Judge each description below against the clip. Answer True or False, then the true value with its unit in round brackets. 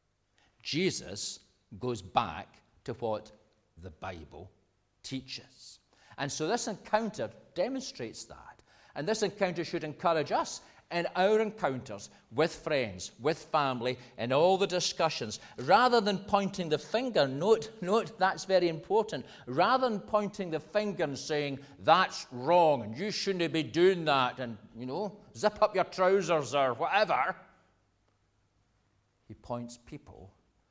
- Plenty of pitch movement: True (8.5 semitones)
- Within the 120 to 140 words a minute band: True (135 wpm)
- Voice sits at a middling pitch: True (150 Hz)